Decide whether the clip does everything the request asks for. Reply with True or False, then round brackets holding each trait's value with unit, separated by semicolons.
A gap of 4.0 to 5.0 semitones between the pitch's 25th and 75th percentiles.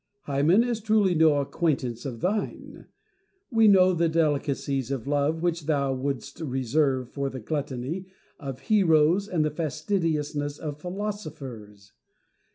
True (4.3 semitones)